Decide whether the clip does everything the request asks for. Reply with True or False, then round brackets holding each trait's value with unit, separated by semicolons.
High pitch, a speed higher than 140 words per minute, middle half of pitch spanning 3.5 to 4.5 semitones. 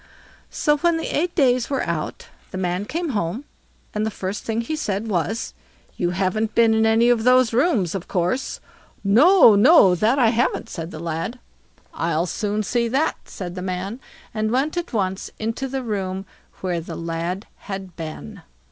False (215 Hz; 175 wpm; 5.3 semitones)